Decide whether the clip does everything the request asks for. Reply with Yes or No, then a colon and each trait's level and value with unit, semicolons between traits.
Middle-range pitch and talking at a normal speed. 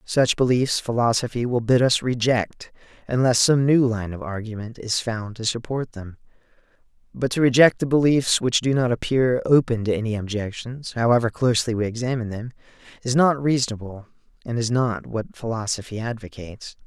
No: low, 120 Hz; average, 160 wpm